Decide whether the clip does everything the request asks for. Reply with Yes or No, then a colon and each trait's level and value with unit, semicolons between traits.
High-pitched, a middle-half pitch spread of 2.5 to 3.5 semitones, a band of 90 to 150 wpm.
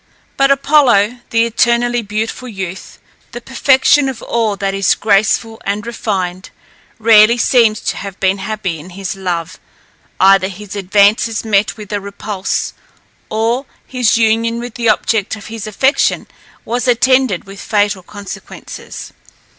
Yes: high, 215 Hz; average, 3.1 semitones; average, 140 wpm